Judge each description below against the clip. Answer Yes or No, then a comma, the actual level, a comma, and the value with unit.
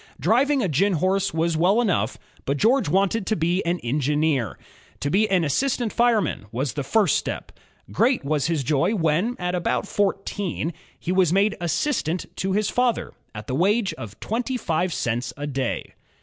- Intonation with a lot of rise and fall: Yes, wide, 6.1 semitones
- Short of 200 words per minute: Yes, average, 170 wpm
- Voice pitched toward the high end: No, medium, 180 Hz